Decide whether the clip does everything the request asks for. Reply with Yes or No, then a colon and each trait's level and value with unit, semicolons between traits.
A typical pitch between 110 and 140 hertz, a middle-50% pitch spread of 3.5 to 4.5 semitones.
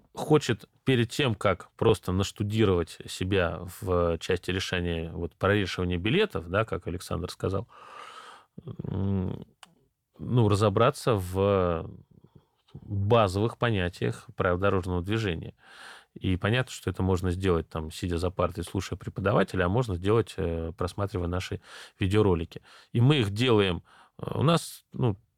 No: very low, 95 Hz; average, 3.8 semitones